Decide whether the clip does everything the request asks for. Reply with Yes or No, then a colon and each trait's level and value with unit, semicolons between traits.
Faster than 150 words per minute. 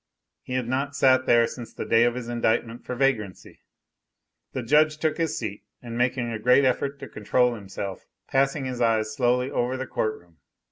Yes: average, 190 wpm